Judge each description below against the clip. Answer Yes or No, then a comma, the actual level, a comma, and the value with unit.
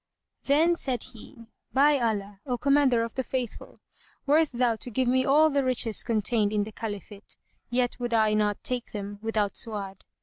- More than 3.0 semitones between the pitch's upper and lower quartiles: Yes, average, 3.6 semitones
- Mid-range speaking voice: No, high, 235 Hz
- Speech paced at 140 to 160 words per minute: No, average, 175 wpm